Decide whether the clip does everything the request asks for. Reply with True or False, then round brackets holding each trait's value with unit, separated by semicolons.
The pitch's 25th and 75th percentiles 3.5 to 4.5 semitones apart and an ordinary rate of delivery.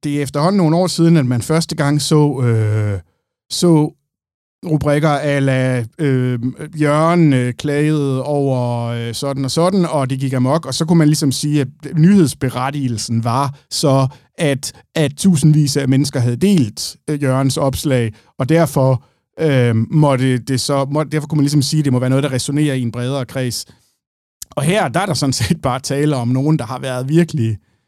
False (3.1 semitones; 185 wpm)